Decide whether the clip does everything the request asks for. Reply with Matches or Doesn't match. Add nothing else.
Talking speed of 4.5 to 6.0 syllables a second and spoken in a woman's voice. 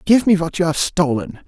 Doesn't match